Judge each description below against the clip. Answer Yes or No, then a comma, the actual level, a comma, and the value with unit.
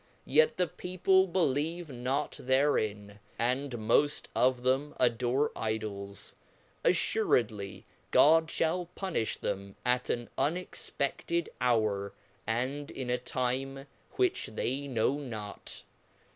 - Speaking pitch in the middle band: No, low, 130 Hz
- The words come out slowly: Yes, slow, 95 wpm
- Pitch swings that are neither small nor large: Yes, average, 4.9 semitones